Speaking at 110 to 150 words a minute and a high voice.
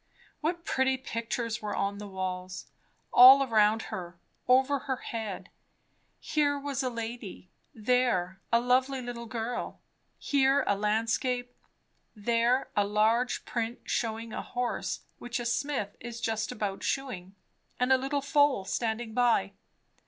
Yes: slow, 135 wpm; high, 235 Hz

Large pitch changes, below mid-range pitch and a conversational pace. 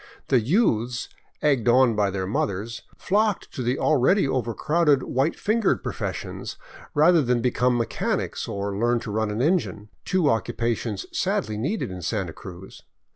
Yes: wide, 5.7 semitones; low, 120 Hz; average, 145 wpm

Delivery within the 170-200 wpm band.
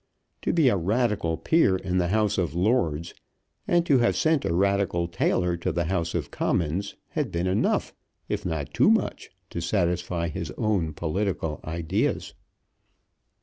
No: average, 155 wpm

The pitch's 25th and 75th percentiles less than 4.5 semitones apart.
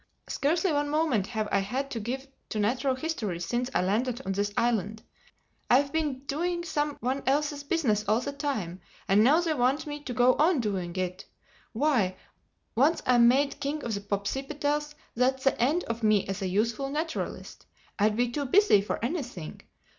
No: wide, 5.5 semitones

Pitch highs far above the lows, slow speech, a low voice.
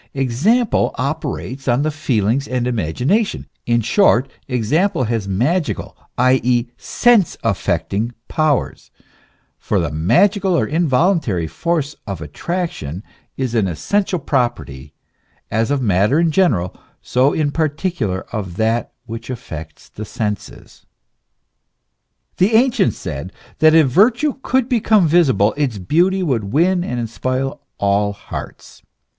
Yes: wide, 7.9 semitones; slow, 125 wpm; low, 130 Hz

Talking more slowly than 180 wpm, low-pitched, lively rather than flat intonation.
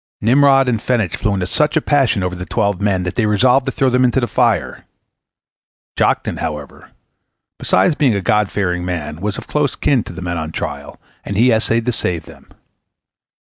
No: average, 195 wpm; low, 105 Hz; wide, 5.8 semitones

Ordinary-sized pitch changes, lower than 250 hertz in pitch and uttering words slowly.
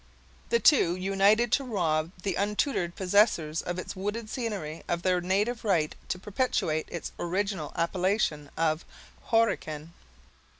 Yes: average, 3.9 semitones; medium, 185 Hz; slow, 130 wpm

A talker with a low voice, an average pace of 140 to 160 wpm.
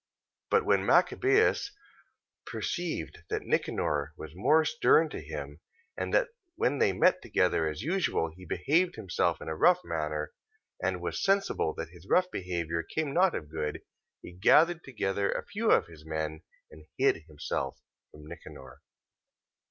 Yes: very low, 90 Hz; average, 155 wpm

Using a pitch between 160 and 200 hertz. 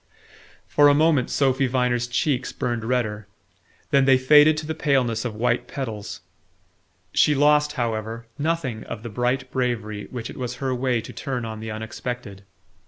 No: low, 125 Hz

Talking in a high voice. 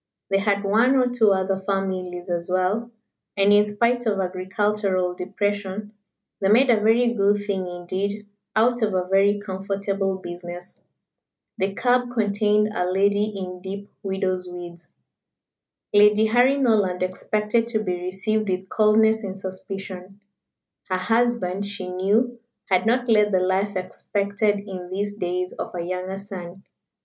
Yes: high, 200 Hz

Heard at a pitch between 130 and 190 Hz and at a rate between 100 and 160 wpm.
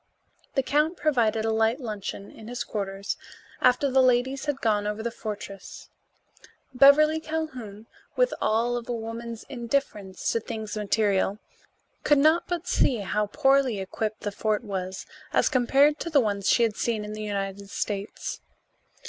No: high, 225 Hz; average, 155 wpm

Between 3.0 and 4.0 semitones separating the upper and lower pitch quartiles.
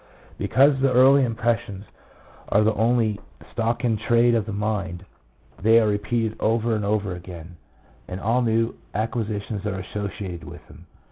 No: narrow, 2.6 semitones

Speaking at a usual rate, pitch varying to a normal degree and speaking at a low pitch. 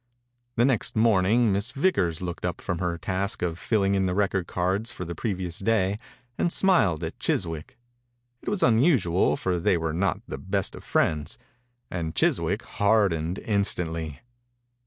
Yes: average, 160 wpm; average, 3.8 semitones; very low, 95 Hz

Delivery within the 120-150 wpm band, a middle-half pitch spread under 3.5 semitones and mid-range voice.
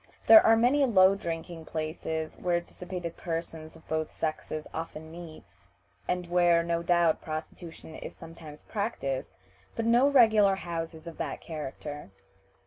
Yes: slow, 135 wpm; average, 2.8 semitones; medium, 170 Hz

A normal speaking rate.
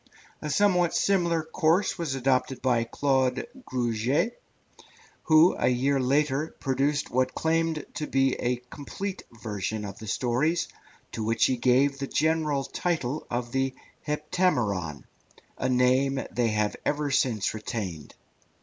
No: slow, 130 wpm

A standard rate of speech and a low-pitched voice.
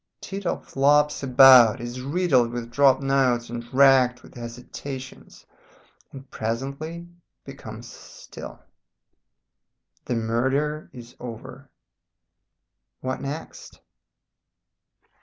No: slow, 85 wpm; low, 130 Hz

